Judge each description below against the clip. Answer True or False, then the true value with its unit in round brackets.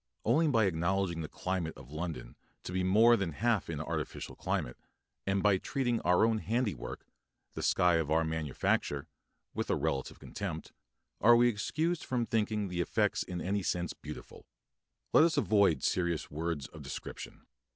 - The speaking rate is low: False (160 wpm)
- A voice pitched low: True (95 Hz)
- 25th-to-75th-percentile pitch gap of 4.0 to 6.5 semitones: True (5.3 semitones)